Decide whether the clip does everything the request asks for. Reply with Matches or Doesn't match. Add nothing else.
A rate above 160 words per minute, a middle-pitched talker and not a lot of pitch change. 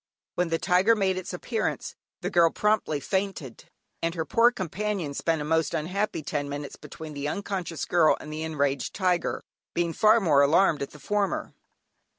Doesn't match